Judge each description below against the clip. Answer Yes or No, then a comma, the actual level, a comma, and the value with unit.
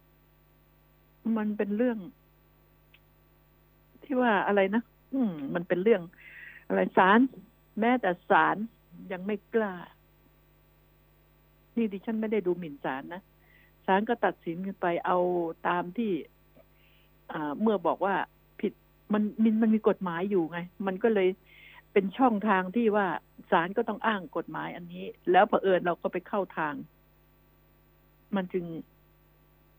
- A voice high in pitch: Yes, high, 195 Hz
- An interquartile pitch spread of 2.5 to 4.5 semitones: Yes, average, 4.0 semitones